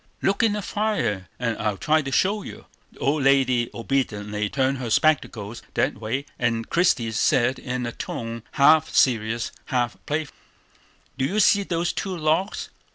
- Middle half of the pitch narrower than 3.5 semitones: No, wide, 5.5 semitones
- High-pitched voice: No, low, 130 Hz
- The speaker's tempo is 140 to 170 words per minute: Yes, average, 160 wpm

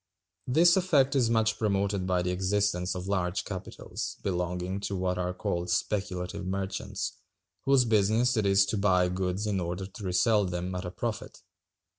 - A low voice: Yes, very low, 95 Hz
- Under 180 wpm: Yes, average, 165 wpm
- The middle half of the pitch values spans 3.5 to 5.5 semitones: No, average, 2.9 semitones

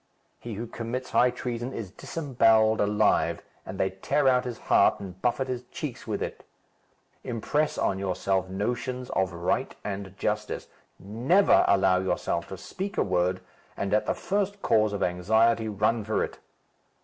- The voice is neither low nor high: No, low, 110 Hz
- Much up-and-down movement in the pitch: No, average, 4.5 semitones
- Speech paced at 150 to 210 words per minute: Yes, average, 160 wpm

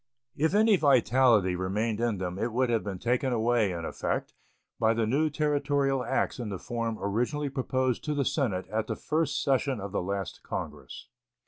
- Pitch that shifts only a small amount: No, average, 5.1 semitones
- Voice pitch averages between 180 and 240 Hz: No, low, 120 Hz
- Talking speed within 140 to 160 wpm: No, average, 185 wpm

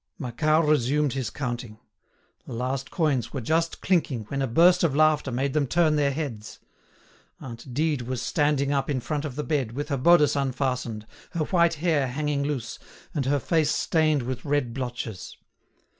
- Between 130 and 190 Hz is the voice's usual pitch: Yes, medium, 140 Hz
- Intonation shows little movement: No, average, 3.4 semitones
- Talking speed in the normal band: Yes, average, 175 wpm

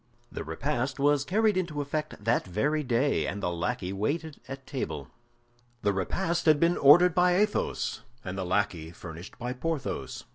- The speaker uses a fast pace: No, average, 160 wpm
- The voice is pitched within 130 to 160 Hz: Yes, low, 135 Hz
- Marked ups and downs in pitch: Yes, wide, 8.4 semitones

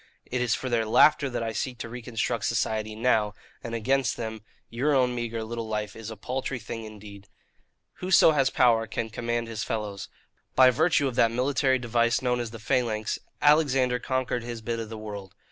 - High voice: No, low, 115 Hz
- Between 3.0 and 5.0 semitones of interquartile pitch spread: No, narrow, 2.5 semitones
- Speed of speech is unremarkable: Yes, average, 190 wpm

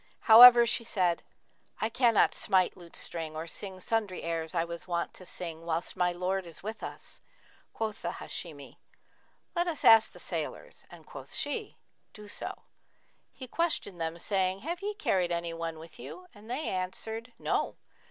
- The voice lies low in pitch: No, medium, 185 Hz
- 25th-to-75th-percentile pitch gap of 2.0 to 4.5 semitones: No, average, 4.9 semitones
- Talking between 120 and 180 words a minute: Yes, average, 165 wpm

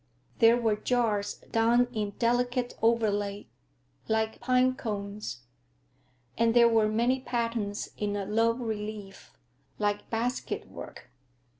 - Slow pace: Yes, slow, 120 wpm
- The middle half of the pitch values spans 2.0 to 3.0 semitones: Yes, narrow, 2.5 semitones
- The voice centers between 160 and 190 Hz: No, high, 225 Hz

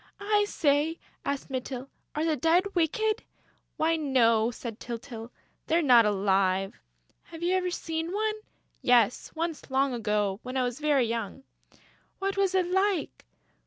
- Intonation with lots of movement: Yes, wide, 6.7 semitones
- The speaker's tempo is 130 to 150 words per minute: Yes, average, 145 wpm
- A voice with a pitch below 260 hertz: No, very high, 280 Hz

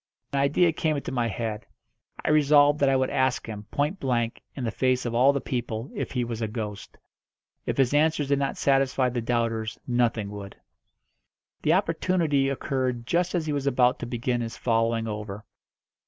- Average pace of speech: Yes, average, 185 wpm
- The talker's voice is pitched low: Yes, low, 125 Hz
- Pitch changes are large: No, average, 3.5 semitones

